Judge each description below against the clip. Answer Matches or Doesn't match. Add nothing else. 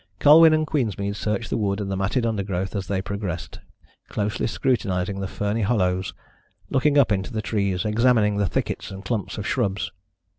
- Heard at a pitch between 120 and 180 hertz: Doesn't match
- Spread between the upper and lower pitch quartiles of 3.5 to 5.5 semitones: Doesn't match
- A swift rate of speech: Doesn't match